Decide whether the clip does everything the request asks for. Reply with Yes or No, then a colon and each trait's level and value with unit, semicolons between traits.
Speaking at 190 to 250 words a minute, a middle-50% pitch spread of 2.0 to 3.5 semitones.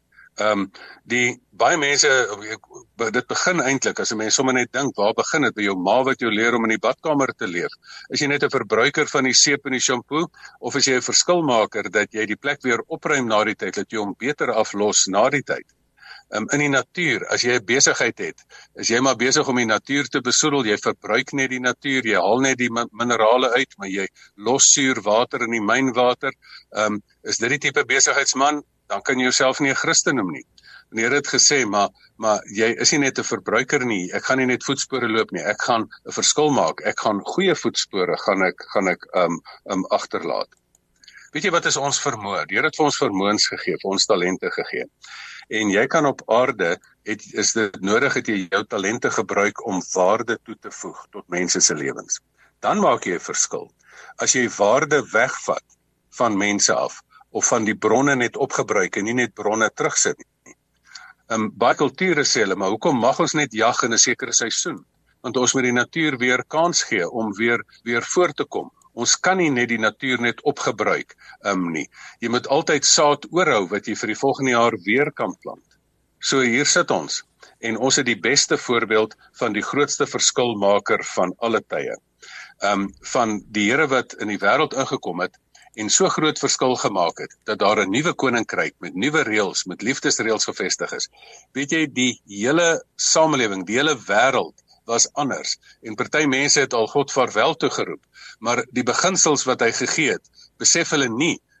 No: average, 200 wpm; average, 4.7 semitones